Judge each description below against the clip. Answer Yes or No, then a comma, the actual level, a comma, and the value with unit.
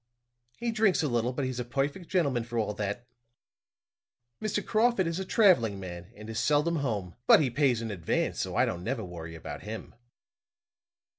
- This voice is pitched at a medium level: No, low, 120 Hz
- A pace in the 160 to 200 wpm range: Yes, average, 180 wpm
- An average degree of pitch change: No, wide, 7.7 semitones